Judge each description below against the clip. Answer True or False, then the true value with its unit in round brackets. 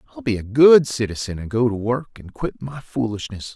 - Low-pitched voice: True (115 Hz)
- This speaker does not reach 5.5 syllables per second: True (5.3 syllables/s)